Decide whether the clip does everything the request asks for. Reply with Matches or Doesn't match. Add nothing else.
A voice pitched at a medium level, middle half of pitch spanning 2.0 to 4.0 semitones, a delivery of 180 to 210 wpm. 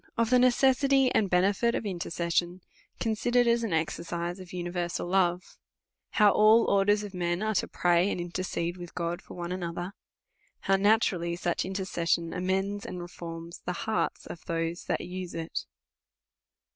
Doesn't match